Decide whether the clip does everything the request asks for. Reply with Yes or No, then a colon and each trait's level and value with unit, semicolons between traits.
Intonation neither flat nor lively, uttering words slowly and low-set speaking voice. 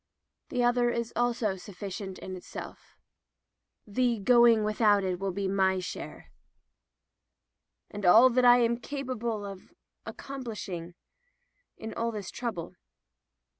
No: average, 3.9 semitones; slow, 120 wpm; high, 215 Hz